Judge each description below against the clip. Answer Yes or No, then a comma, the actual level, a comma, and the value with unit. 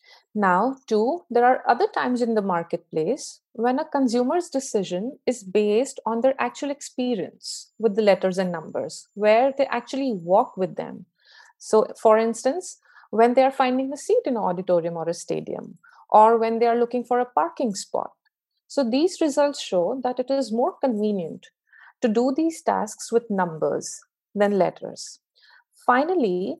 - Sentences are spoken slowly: No, average, 160 wpm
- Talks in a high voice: Yes, high, 245 Hz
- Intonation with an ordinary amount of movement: Yes, average, 4.8 semitones